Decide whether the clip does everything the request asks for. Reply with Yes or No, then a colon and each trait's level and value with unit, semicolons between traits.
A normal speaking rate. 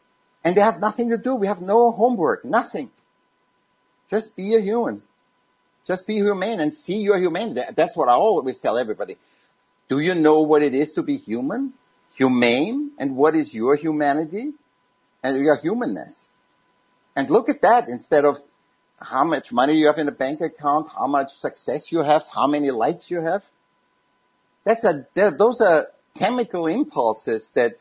Yes: average, 170 wpm